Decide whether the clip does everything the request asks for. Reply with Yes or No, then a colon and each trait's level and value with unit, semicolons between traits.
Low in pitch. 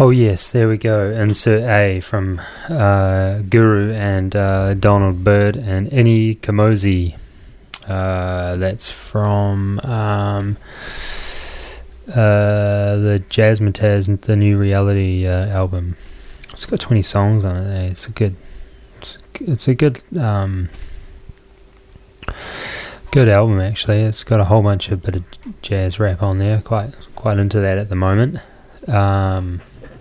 Yes: low, 100 Hz